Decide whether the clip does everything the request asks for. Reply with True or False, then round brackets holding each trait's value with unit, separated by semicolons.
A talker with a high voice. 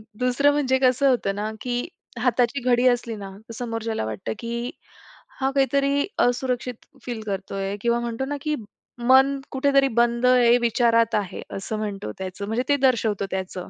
True (240 Hz)